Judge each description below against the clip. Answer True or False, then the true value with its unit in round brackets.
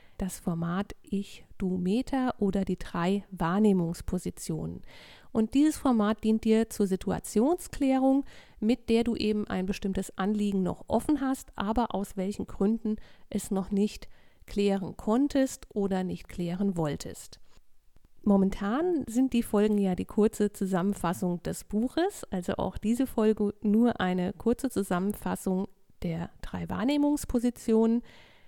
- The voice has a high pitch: True (210 Hz)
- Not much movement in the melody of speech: False (3.6 semitones)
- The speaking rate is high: False (125 wpm)